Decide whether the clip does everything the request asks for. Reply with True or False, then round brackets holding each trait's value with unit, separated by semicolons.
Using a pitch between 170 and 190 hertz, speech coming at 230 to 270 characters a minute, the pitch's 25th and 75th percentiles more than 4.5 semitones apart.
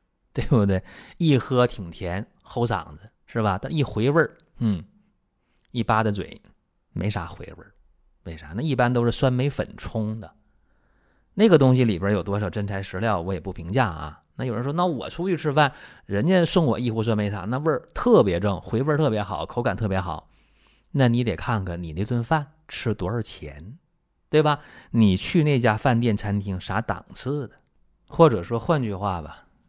False (110 Hz; 260 characters per minute; 5.5 semitones)